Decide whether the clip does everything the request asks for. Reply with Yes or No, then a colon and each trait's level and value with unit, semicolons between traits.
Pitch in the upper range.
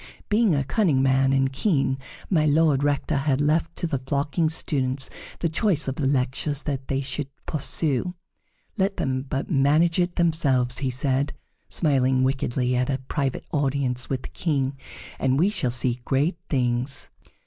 No: medium, 140 Hz